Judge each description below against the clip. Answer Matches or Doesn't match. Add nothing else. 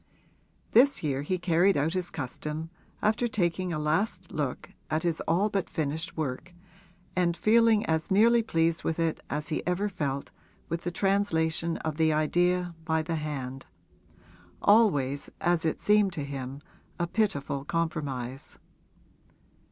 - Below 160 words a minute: Matches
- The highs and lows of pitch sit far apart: Doesn't match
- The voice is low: Doesn't match